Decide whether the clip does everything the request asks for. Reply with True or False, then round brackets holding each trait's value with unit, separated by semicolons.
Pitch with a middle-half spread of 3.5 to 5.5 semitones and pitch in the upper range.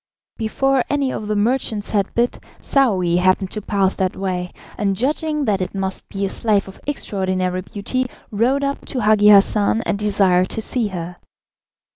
True (4.0 semitones; 205 Hz)